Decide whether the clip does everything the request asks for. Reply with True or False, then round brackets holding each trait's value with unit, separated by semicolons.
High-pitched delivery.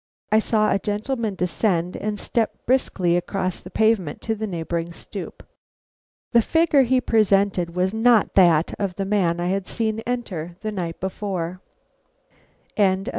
True (200 Hz)